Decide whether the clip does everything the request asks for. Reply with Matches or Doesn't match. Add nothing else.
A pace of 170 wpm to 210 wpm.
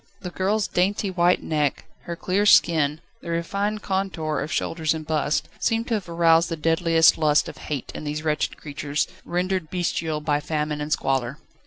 Matches